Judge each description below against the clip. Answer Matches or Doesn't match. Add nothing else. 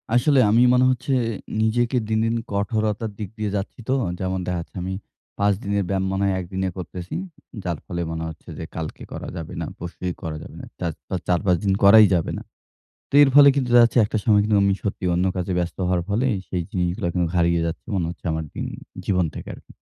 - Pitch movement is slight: Doesn't match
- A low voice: Matches